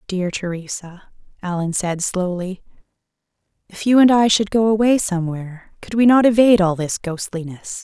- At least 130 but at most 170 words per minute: Yes, average, 155 wpm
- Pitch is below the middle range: No, high, 195 Hz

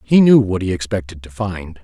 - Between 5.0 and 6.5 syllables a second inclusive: Yes, 5.2 syllables/s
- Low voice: Yes, low, 100 Hz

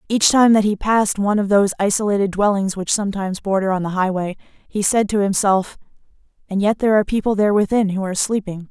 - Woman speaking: Yes, female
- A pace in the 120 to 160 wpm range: No, fast, 205 wpm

